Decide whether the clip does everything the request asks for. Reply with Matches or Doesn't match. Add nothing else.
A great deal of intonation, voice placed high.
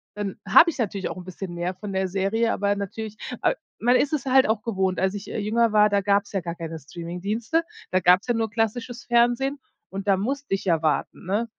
Doesn't match